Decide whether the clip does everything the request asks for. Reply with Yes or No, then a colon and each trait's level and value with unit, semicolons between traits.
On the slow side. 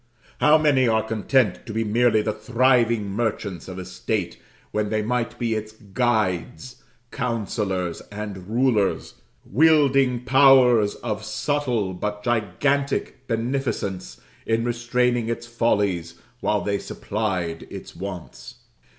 Yes: slow, 120 wpm